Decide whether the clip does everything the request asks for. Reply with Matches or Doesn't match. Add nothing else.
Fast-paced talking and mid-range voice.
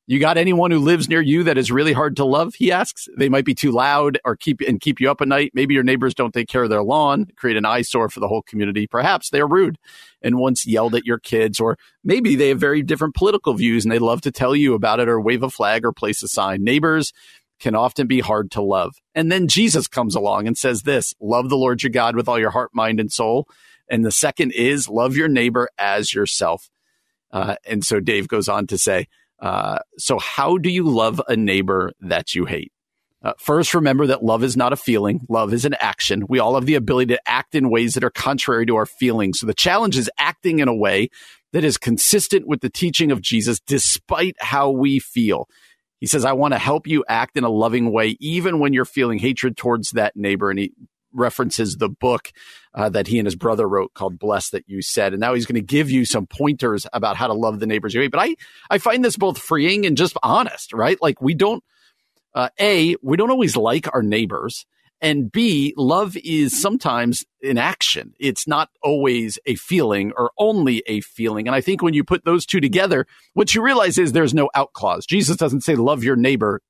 Doesn't match